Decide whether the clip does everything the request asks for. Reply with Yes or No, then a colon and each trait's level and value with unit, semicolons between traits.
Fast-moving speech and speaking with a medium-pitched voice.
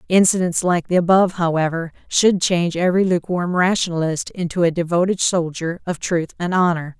No: average, 155 wpm; medium, 175 Hz